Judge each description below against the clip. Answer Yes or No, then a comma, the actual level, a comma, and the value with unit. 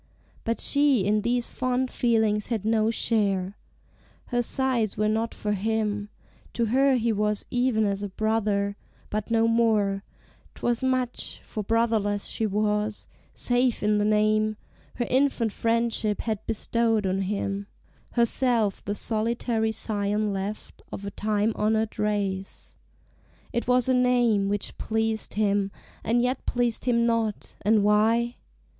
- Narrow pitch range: Yes, narrow, 2.1 semitones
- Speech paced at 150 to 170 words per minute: No, average, 140 wpm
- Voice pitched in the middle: No, high, 220 Hz